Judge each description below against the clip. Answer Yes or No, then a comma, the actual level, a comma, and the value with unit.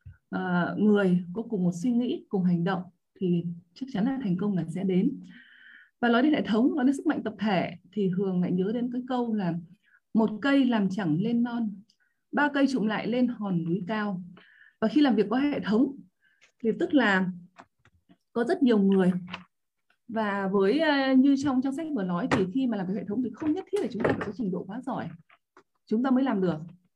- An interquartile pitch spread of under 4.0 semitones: No, wide, 5.6 semitones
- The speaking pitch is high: Yes, high, 215 Hz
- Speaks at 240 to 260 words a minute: No, average, 220 wpm